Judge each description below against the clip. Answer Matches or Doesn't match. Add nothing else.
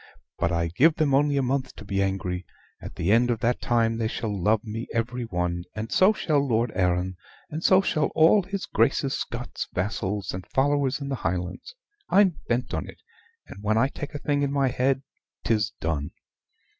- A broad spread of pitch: Matches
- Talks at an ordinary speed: Matches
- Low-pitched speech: Matches